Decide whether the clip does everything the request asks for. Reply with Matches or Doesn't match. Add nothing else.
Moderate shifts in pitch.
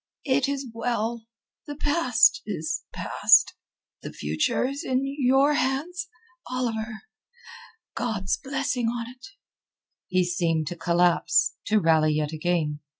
Doesn't match